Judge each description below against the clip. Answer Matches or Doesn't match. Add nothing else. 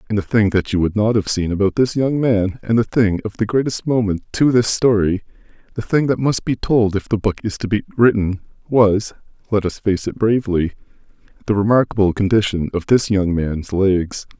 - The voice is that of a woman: Doesn't match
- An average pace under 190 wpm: Doesn't match